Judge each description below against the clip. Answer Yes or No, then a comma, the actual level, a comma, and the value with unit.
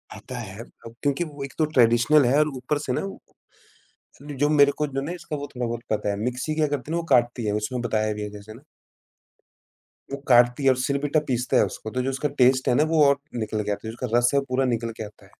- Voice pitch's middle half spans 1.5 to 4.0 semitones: Yes, average, 3.6 semitones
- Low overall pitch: Yes, low, 125 Hz